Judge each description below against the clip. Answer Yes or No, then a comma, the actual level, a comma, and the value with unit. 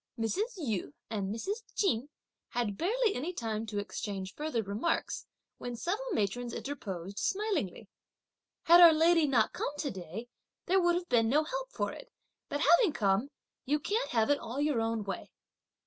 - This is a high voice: Yes, very high, 265 Hz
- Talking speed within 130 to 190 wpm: Yes, average, 170 wpm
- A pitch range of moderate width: No, wide, 8.1 semitones